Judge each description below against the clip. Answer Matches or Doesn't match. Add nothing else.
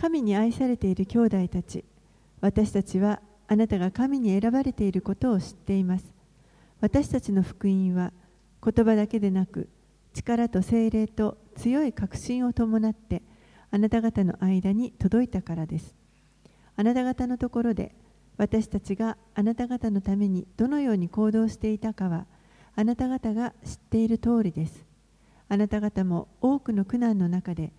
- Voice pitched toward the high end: Matches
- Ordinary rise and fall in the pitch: Matches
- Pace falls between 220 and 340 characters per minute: Matches